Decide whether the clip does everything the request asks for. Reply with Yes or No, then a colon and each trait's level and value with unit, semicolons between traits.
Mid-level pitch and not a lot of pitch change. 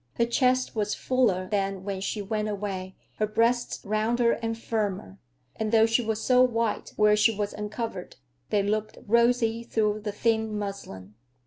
No: high, 215 Hz; narrow, 2.1 semitones